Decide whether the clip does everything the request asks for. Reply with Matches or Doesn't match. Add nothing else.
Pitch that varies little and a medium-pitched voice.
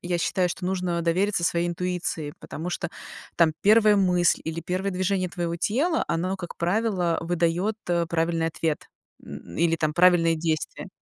Matches